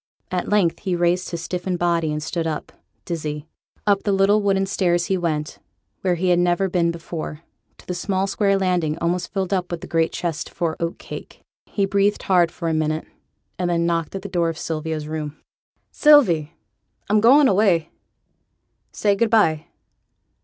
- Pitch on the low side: No, medium, 175 Hz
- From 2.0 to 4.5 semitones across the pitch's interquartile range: Yes, average, 2.9 semitones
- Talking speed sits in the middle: Yes, average, 180 wpm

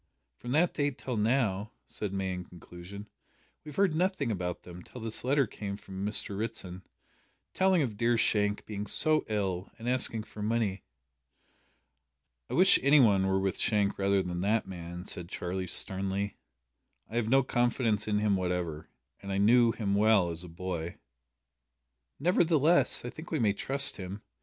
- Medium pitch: No, low, 105 Hz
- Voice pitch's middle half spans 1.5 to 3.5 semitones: No, average, 4.4 semitones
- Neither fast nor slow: Yes, average, 170 wpm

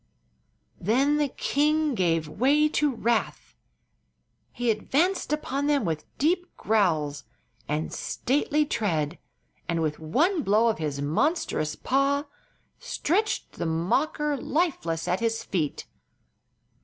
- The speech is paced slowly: Yes, slow, 115 wpm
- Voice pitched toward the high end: Yes, high, 235 Hz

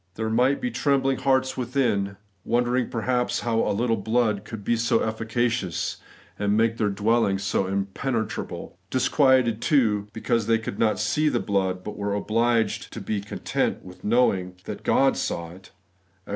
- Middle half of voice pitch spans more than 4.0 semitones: No, average, 3.3 semitones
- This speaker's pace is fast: No, average, 170 wpm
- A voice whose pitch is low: Yes, low, 115 Hz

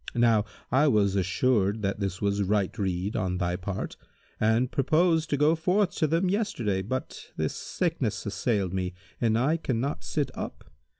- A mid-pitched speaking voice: No, low, 110 Hz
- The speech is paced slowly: No, average, 165 wpm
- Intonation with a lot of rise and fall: Yes, wide, 7.2 semitones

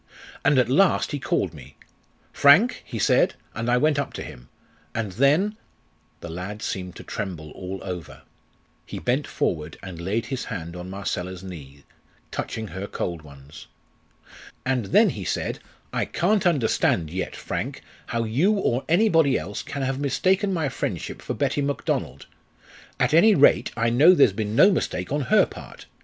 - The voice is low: Yes, low, 115 Hz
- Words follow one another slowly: No, average, 170 wpm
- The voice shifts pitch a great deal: Yes, wide, 8.0 semitones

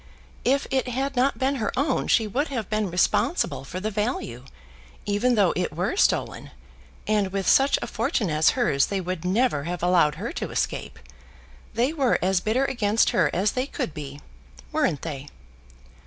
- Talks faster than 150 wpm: Yes, average, 175 wpm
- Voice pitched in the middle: No, high, 210 Hz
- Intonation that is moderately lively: No, wide, 6.4 semitones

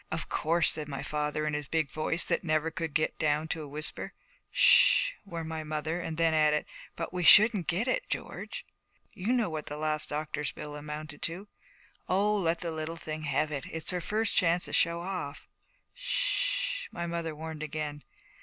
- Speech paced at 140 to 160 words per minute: No, average, 195 wpm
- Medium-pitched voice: Yes, medium, 160 Hz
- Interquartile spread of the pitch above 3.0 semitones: No, average, 2.7 semitones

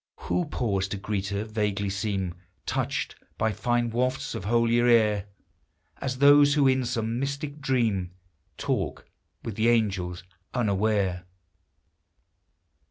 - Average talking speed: No, slow, 120 wpm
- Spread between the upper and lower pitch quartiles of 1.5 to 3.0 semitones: No, average, 4.1 semitones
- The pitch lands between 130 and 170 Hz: No, low, 110 Hz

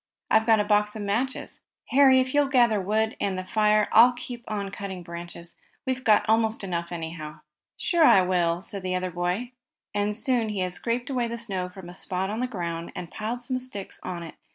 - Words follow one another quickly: Yes, fast, 215 wpm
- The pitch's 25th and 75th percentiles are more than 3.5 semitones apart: Yes, average, 4.5 semitones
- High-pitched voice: Yes, high, 210 Hz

